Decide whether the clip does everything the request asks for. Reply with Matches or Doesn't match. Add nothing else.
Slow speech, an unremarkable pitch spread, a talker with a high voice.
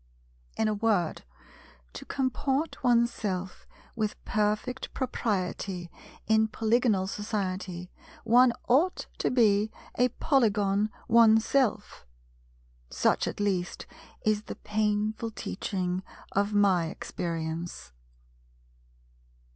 Matches